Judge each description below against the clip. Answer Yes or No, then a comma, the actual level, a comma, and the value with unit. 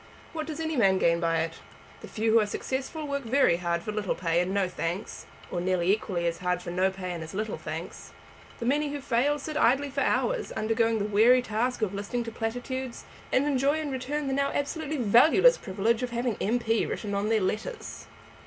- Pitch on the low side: No, high, 225 Hz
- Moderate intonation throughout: No, wide, 6.3 semitones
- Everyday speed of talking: No, fast, 210 wpm